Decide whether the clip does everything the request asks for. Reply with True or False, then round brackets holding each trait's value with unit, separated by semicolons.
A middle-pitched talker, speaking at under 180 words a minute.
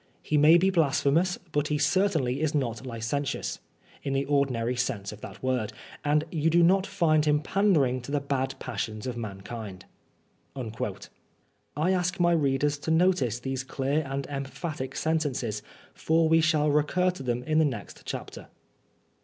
True (145 Hz; 160 wpm)